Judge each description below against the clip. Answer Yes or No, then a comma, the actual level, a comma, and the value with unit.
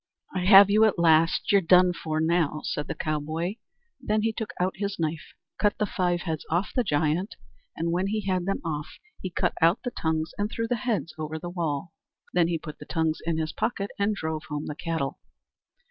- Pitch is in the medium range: Yes, medium, 170 Hz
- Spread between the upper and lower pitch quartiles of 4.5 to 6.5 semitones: No, average, 3.9 semitones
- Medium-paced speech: No, fast, 210 wpm